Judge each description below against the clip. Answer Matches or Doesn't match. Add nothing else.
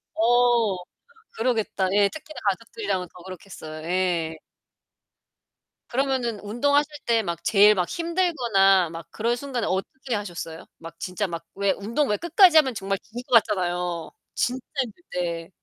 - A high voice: Matches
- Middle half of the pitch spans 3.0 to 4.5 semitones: Doesn't match